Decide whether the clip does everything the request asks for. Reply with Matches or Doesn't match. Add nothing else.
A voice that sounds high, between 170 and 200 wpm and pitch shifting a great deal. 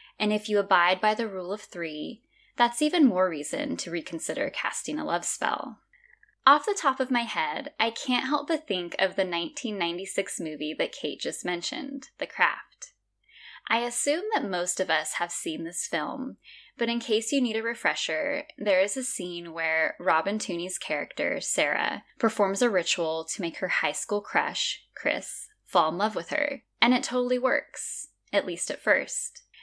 Matches